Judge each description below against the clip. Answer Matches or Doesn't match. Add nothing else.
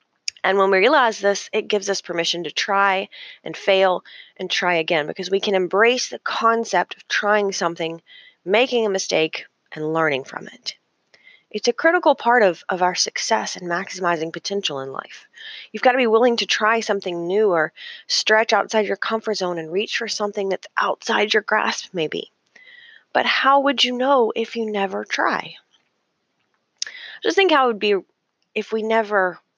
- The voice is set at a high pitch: Matches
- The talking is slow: Doesn't match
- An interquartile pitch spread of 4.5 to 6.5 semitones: Doesn't match